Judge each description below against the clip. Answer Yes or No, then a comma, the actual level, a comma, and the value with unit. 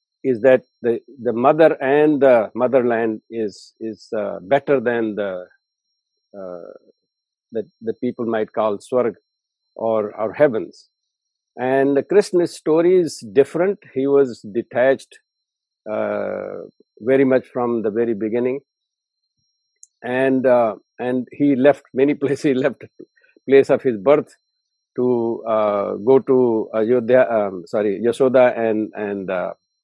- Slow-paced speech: Yes, slow, 130 wpm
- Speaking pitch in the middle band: No, low, 130 Hz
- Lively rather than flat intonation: No, average, 3.7 semitones